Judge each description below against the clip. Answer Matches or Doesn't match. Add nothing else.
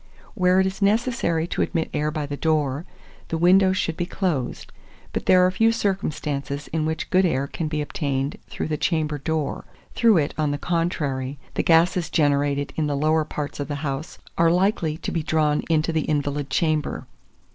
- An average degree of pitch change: Matches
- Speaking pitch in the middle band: Matches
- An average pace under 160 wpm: Doesn't match